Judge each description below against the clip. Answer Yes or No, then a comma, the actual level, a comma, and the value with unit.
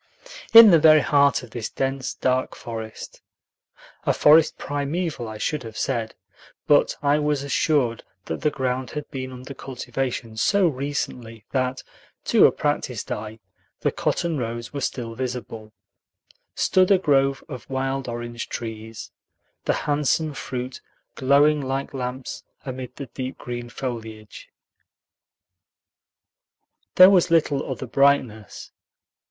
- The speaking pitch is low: Yes, low, 130 Hz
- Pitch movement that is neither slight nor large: Yes, average, 3.4 semitones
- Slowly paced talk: Yes, slow, 130 wpm